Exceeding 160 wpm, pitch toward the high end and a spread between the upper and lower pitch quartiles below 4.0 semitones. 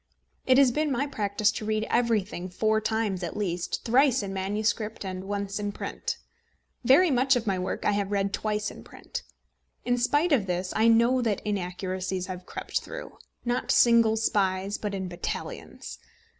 Yes: average, 170 wpm; high, 210 Hz; average, 3.6 semitones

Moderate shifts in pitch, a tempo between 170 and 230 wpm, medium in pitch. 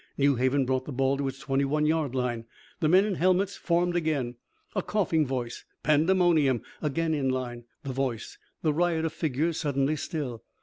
Yes: average, 3.8 semitones; average, 180 wpm; medium, 145 Hz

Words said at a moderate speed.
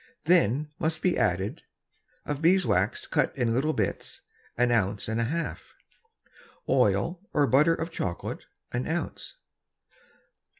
No: slow, 130 wpm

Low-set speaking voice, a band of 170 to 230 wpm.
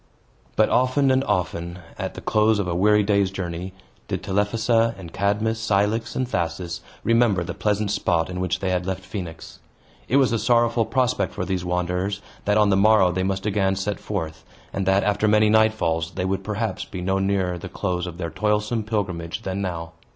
Yes: low, 100 Hz; average, 195 wpm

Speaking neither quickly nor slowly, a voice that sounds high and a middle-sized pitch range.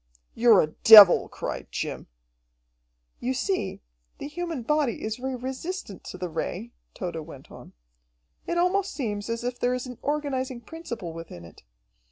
No: average, 155 wpm; high, 245 Hz; wide, 6.3 semitones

